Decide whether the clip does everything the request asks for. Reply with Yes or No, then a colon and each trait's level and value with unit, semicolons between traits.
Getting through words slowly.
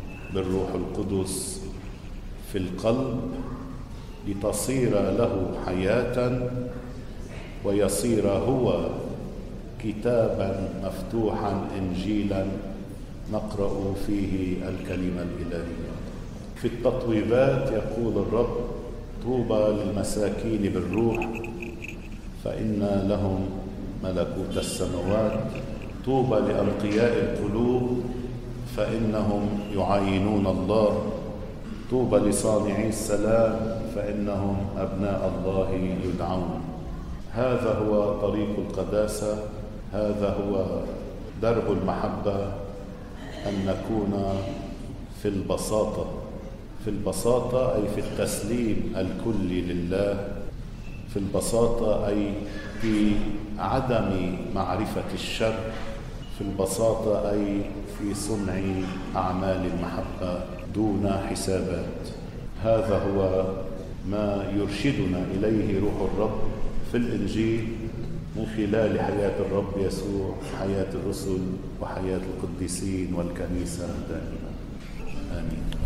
Yes: slow, 75 wpm